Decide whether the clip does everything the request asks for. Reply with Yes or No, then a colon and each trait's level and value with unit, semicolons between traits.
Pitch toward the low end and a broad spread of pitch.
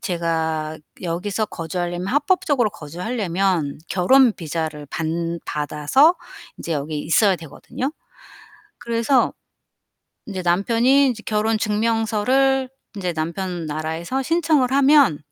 No: high, 190 Hz; wide, 7.2 semitones